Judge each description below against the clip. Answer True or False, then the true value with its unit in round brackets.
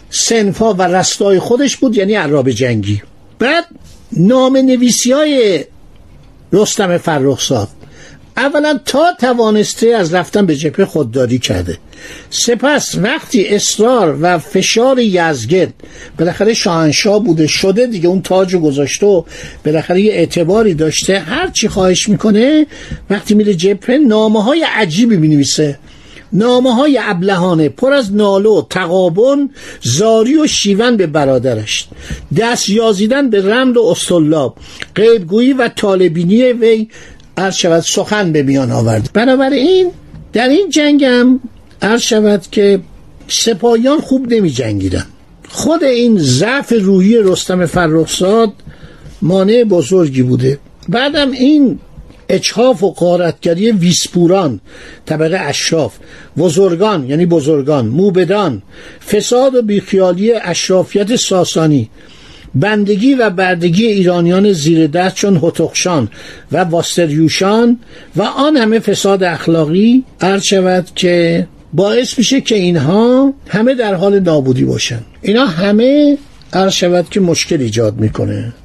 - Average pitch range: False (5.7 semitones)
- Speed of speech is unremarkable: True (115 wpm)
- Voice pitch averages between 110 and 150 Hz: False (195 Hz)